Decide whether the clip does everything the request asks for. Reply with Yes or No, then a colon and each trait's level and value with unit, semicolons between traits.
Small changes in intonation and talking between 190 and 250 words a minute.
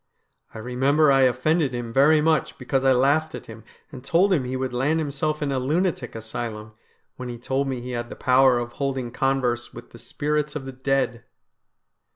No: average, 3.2 semitones; average, 195 wpm